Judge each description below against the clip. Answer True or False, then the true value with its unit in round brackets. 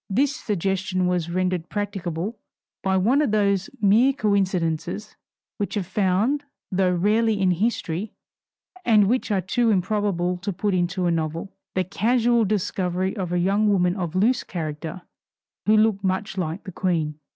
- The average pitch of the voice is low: False (190 Hz)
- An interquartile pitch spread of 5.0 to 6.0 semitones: False (2.9 semitones)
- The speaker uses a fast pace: False (150 wpm)